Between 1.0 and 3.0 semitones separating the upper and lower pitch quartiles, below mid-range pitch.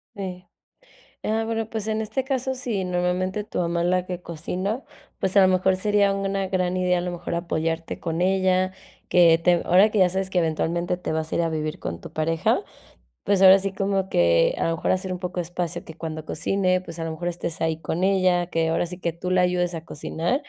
No: narrow, 2.4 semitones; medium, 180 Hz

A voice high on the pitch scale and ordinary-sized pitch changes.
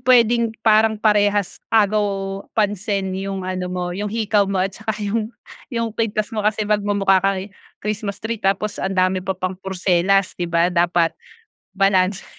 No: high, 200 Hz; narrow, 2.2 semitones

